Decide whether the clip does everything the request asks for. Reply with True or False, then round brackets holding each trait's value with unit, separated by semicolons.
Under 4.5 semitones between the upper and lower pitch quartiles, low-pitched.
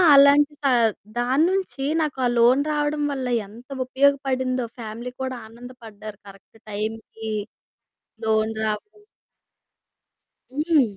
False (4.1 semitones; 255 Hz)